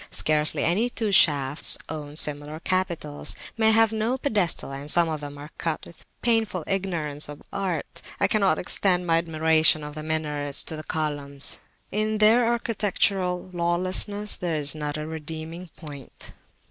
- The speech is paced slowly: No, average, 160 wpm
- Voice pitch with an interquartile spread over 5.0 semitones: No, average, 4.5 semitones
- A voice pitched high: No, medium, 165 Hz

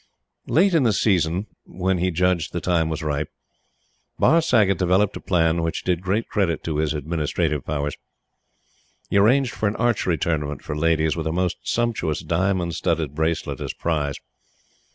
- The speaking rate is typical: Yes, average, 165 wpm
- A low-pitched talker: Yes, very low, 85 Hz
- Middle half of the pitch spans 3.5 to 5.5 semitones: Yes, average, 3.8 semitones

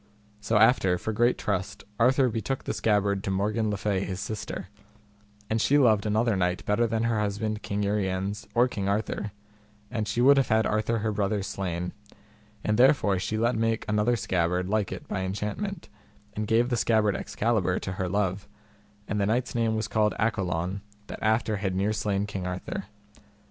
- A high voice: No, low, 105 Hz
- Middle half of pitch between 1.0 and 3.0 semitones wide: Yes, narrow, 2.4 semitones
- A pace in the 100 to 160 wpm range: No, average, 180 wpm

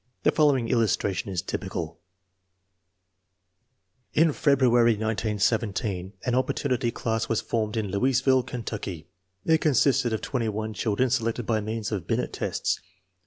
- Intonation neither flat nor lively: Yes, average, 3.3 semitones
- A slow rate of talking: Yes, slow, 120 wpm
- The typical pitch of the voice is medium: No, low, 115 Hz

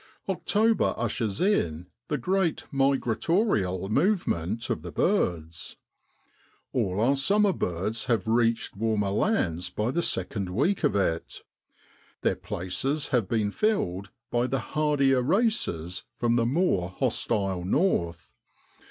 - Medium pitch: No, low, 115 Hz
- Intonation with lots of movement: Yes, wide, 8.7 semitones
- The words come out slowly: Yes, slow, 120 wpm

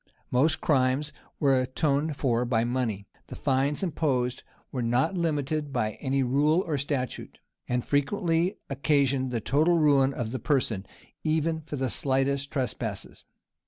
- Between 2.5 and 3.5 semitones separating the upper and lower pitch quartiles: Yes, average, 3.1 semitones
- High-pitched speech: No, medium, 140 Hz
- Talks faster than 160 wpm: No, average, 145 wpm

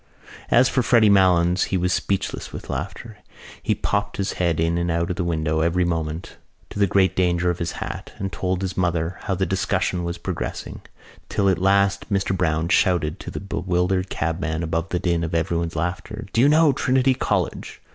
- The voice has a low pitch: Yes, very low, 90 Hz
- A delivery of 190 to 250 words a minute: Yes, average, 195 wpm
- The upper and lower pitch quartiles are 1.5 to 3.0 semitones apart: Yes, narrow, 2.6 semitones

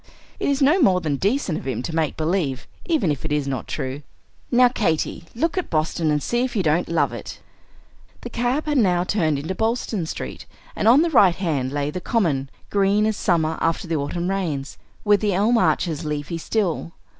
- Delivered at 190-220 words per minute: Yes, average, 200 wpm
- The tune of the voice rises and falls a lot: Yes, wide, 6.3 semitones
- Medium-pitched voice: Yes, medium, 175 Hz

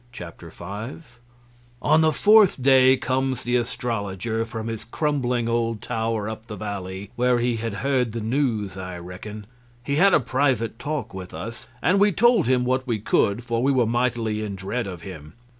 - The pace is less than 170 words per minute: No, average, 180 wpm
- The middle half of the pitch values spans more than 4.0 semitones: No, average, 3.6 semitones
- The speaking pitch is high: No, low, 115 Hz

